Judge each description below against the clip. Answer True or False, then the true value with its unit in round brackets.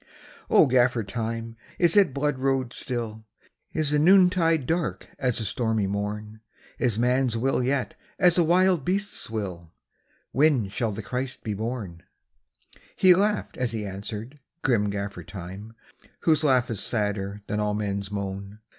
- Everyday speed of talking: True (165 wpm)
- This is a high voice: False (115 Hz)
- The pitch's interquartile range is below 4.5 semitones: False (5.2 semitones)